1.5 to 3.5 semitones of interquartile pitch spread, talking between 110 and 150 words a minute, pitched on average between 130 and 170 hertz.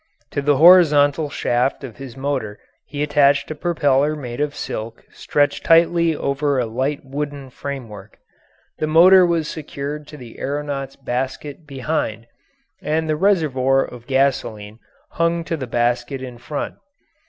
Yes: average, 2.9 semitones; average, 140 wpm; medium, 140 Hz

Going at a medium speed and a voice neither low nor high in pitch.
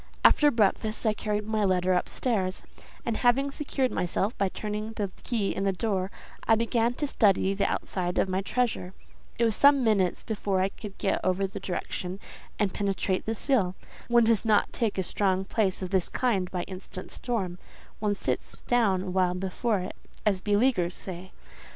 No: average, 175 wpm; high, 200 Hz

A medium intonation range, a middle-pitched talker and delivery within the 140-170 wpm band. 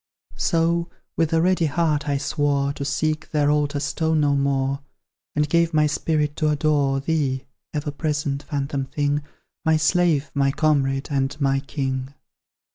No: narrow, 2.0 semitones; medium, 145 Hz; average, 150 wpm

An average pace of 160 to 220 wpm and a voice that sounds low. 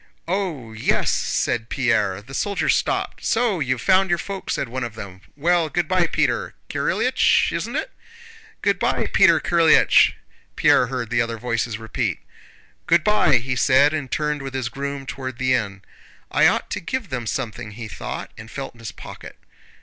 Yes: average, 170 wpm; low, 130 Hz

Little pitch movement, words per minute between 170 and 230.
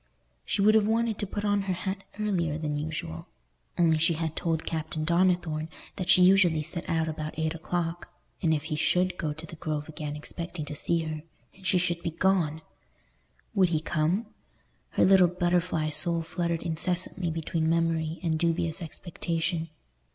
Yes: narrow, 2.3 semitones; average, 175 wpm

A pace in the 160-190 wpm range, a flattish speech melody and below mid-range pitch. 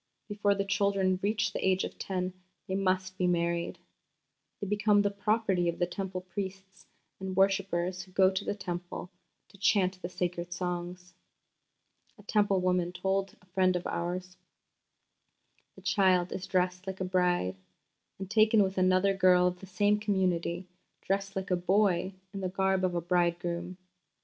No: average, 165 wpm; narrow, 1.6 semitones; medium, 185 Hz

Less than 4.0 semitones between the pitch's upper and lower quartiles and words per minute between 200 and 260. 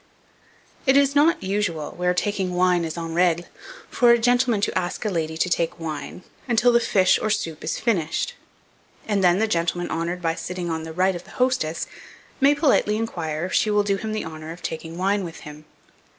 No: average, 4.7 semitones; fast, 205 wpm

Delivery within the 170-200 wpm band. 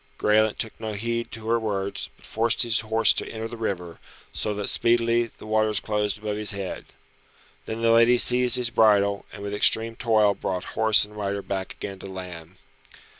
Yes: average, 190 wpm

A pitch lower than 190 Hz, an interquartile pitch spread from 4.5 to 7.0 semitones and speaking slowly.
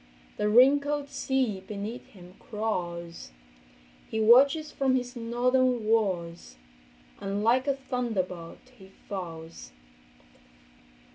No: high, 225 Hz; average, 5.3 semitones; slow, 95 wpm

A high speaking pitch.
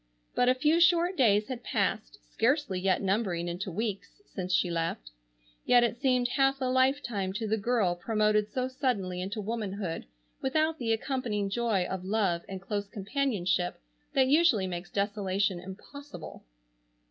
Yes: high, 215 Hz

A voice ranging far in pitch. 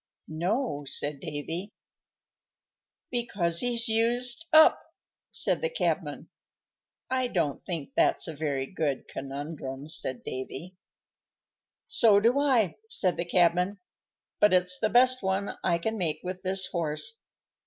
Yes: wide, 6.8 semitones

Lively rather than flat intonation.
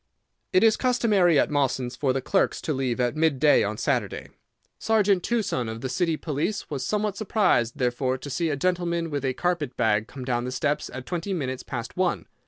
Yes: wide, 6.0 semitones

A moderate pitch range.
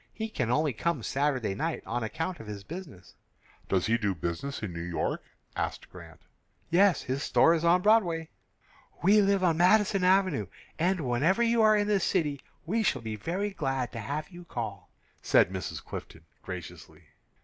No: wide, 8.7 semitones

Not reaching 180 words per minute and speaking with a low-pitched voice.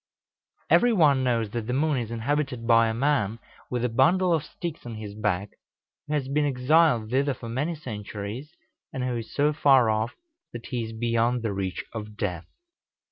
No: average, 190 wpm; low, 120 Hz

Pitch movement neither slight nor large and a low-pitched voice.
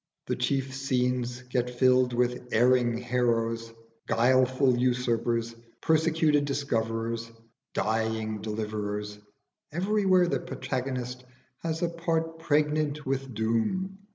Yes: average, 4.1 semitones; low, 125 Hz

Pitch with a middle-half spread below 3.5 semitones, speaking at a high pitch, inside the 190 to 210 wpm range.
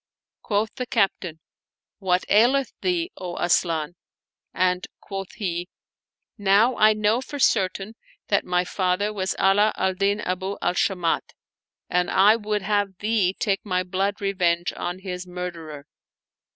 No: narrow, 2.6 semitones; high, 195 Hz; average, 140 wpm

